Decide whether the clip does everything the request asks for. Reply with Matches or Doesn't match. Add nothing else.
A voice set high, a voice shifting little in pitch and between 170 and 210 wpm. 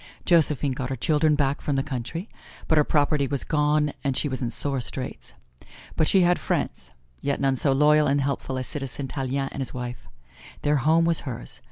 Doesn't match